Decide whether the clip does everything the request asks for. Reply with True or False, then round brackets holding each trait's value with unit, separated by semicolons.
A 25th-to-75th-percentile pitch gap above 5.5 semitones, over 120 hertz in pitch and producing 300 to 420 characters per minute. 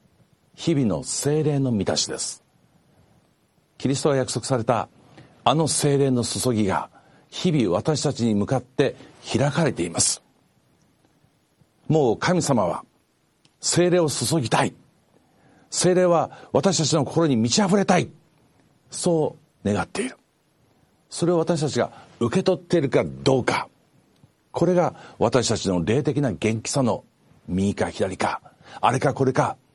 False (5.9 semitones; 140 Hz; 245 characters per minute)